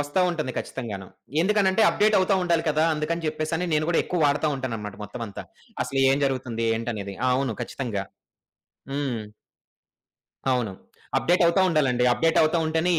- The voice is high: No, medium, 145 Hz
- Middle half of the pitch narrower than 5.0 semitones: No, wide, 5.4 semitones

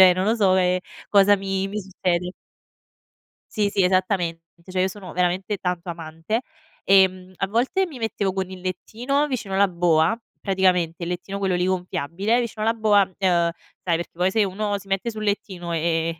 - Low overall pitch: No, high, 190 Hz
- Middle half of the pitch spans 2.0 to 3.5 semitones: Yes, narrow, 2.4 semitones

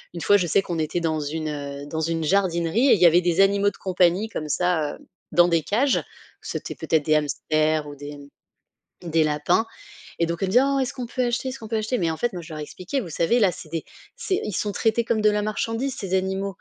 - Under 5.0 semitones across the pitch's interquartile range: No, average, 5.3 semitones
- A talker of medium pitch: Yes, medium, 180 Hz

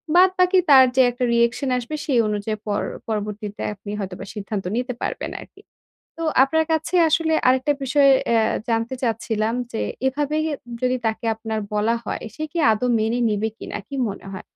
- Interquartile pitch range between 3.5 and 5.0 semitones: Yes, average, 4.2 semitones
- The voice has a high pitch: Yes, high, 235 Hz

